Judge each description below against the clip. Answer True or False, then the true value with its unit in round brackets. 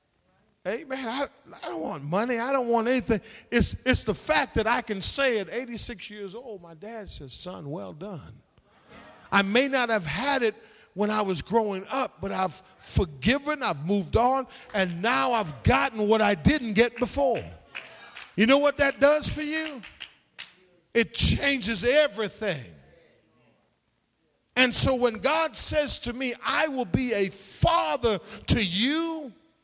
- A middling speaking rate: True (160 wpm)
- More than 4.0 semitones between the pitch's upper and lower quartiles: True (4.9 semitones)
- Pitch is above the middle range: True (230 Hz)